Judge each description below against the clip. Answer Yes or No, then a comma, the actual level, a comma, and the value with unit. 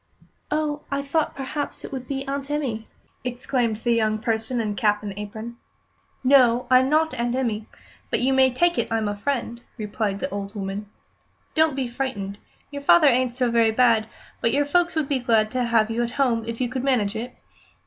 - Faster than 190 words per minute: Yes, average, 200 wpm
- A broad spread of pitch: No, average, 3.7 semitones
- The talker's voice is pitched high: Yes, high, 245 Hz